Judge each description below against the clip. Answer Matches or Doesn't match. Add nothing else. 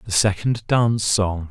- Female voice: Doesn't match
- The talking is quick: Doesn't match